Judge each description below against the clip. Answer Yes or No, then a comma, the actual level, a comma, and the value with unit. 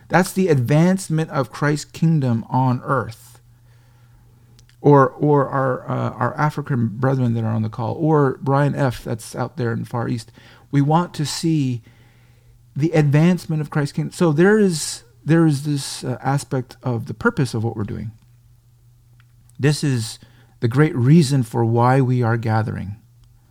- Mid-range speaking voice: No, low, 125 Hz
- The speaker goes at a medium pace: Yes, average, 165 wpm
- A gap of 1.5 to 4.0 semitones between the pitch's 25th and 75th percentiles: Yes, average, 3.7 semitones